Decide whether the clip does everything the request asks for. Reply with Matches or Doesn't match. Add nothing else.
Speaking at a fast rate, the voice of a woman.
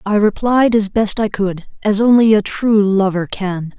Doesn't match